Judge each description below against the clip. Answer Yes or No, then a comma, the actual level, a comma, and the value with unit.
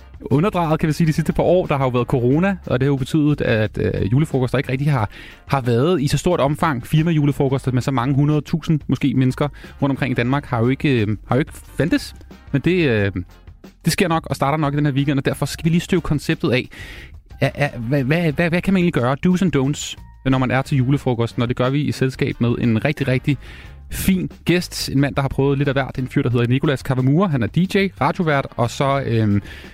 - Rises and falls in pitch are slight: No, average, 3.8 semitones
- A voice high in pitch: No, medium, 140 Hz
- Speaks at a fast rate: Yes, fast, 235 wpm